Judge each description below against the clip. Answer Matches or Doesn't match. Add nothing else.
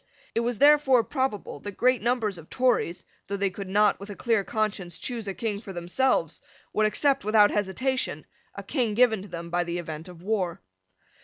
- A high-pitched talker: Matches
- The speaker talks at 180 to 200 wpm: Matches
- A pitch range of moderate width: Matches